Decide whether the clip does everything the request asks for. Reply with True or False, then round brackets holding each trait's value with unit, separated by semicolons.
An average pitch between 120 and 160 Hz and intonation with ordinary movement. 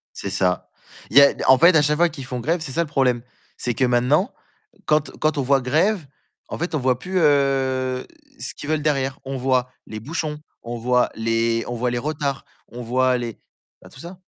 True (130 Hz; 3.5 semitones)